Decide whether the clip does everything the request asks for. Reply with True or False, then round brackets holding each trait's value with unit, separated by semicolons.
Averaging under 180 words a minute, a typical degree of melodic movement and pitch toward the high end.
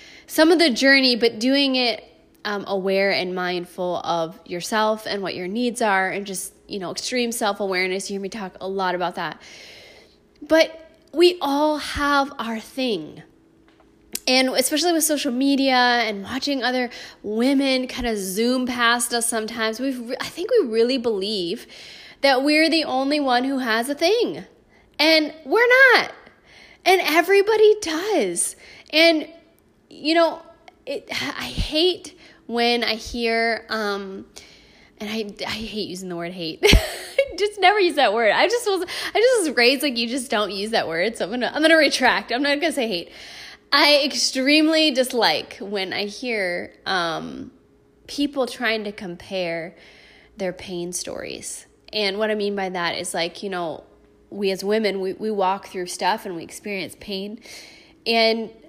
False (165 wpm; 7.4 semitones; 240 Hz)